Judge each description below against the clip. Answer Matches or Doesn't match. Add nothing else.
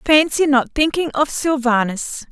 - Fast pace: Doesn't match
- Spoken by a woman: Matches